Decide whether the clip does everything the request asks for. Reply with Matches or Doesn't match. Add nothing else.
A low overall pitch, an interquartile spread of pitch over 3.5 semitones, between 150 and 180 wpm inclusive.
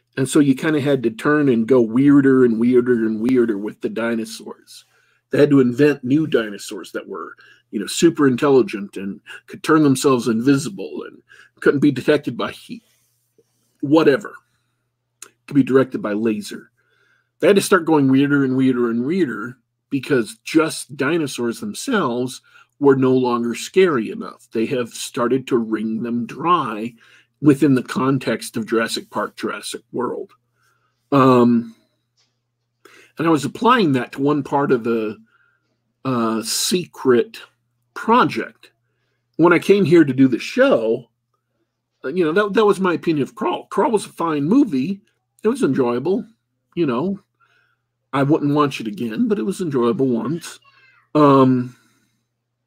Matches